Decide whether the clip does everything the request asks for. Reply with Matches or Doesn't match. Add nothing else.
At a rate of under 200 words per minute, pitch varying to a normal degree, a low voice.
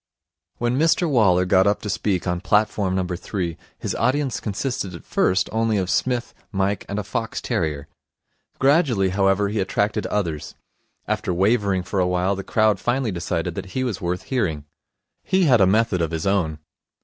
Matches